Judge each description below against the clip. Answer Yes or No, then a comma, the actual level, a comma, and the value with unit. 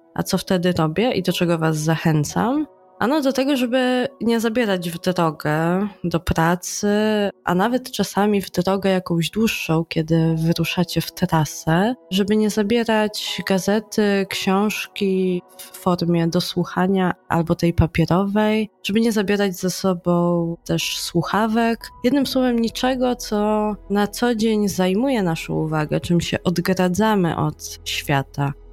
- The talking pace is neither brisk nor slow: Yes, average, 130 wpm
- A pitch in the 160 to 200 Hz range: Yes, high, 190 Hz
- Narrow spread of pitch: No, average, 4.0 semitones